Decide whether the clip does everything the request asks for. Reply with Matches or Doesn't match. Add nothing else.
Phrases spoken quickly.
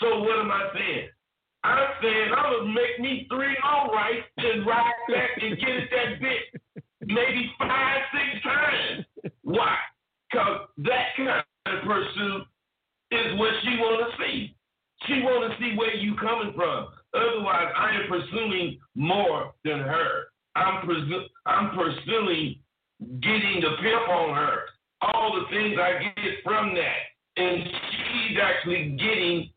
Doesn't match